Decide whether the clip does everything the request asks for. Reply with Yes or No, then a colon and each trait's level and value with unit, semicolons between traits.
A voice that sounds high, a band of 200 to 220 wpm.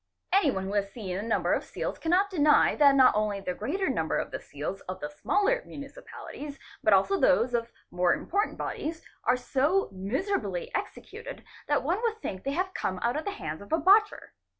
Yes: very high, 275 Hz; fast, 205 wpm